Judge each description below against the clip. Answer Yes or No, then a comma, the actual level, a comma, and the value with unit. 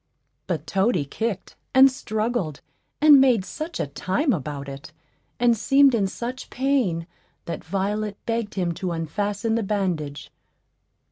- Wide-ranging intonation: Yes, wide, 6.2 semitones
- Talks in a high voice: Yes, high, 205 Hz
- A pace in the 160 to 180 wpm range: No, slow, 135 wpm